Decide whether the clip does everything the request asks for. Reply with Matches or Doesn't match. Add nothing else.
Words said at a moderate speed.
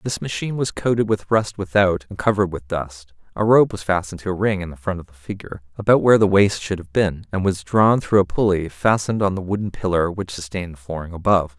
Doesn't match